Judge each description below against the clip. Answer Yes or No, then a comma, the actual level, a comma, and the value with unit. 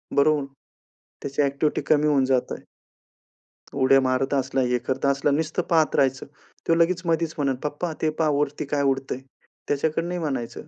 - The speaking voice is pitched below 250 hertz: Yes, medium, 140 Hz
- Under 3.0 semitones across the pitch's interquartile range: Yes, narrow, 2.5 semitones